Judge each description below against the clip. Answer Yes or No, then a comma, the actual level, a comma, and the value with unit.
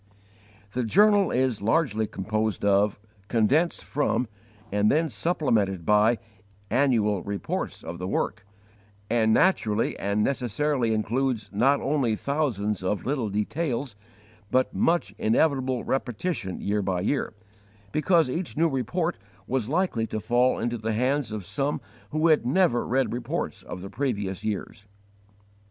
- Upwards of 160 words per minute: No, slow, 135 wpm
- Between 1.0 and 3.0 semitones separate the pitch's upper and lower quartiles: No, average, 5.3 semitones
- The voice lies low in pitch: Yes, low, 120 Hz